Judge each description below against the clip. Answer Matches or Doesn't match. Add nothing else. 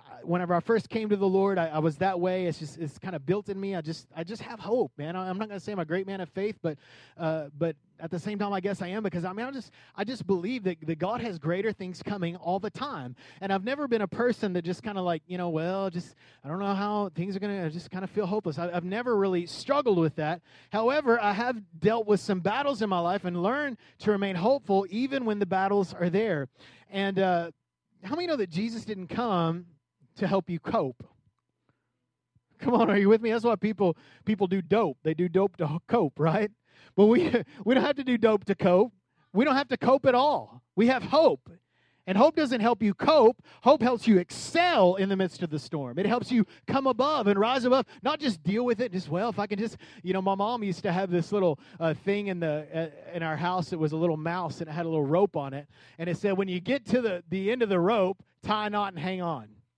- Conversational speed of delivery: Doesn't match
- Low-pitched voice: Doesn't match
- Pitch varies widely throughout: Doesn't match